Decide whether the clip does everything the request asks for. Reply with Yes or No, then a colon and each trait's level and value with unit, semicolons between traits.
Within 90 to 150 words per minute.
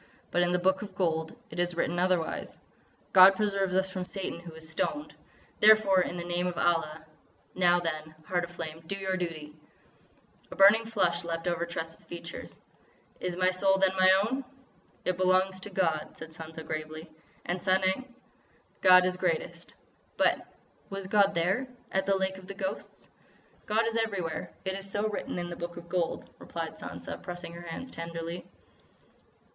No: average, 165 wpm